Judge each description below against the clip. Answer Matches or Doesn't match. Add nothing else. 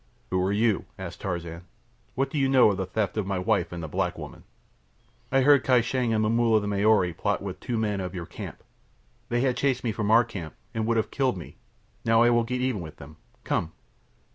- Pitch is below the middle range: Matches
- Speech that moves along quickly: Matches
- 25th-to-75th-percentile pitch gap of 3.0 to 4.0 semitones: Doesn't match